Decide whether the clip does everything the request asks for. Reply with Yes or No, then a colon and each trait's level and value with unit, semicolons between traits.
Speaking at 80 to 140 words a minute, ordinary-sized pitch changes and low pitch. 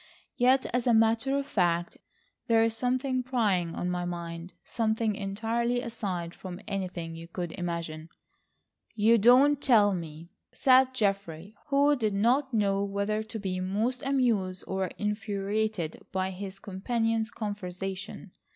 No: slow, 135 wpm; average, 4.2 semitones; high, 205 Hz